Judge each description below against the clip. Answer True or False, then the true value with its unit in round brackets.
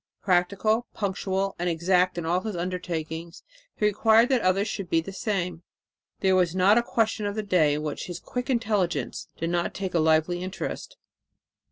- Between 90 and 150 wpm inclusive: False (180 wpm)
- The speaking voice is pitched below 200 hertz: True (185 Hz)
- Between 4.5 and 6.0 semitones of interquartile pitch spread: False (3.3 semitones)